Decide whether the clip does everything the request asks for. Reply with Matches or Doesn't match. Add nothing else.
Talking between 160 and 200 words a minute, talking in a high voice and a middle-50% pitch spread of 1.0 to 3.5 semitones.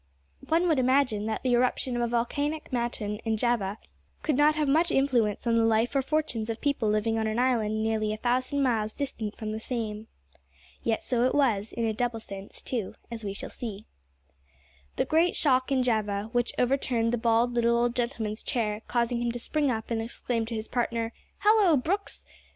Matches